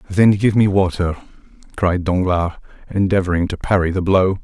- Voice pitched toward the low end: Yes, very low, 95 Hz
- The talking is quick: No, average, 150 wpm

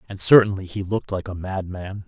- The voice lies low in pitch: Yes, very low, 95 Hz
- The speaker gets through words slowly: No, fast, 205 wpm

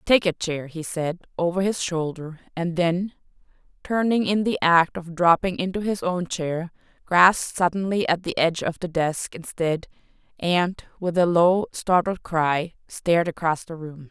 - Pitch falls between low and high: Yes, medium, 175 Hz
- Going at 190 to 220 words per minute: No, average, 160 wpm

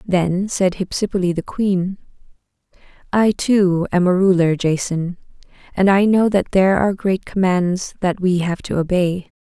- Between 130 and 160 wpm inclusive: Yes, average, 155 wpm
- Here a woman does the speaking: Yes, female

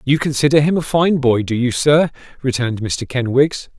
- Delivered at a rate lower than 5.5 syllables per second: Yes, 5.1 syllables/s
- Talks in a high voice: No, low, 135 Hz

